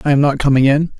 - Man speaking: Yes, male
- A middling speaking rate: No, fast, 305 wpm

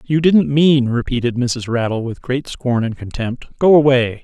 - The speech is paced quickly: No, average, 185 wpm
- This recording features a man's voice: Yes, male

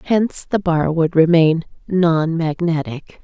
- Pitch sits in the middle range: Yes, medium, 165 Hz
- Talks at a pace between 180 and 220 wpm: No, slow, 130 wpm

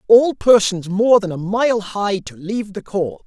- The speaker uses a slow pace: No, average, 200 wpm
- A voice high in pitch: Yes, high, 205 Hz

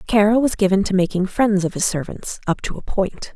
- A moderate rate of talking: No, fast, 215 wpm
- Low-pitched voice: No, high, 195 Hz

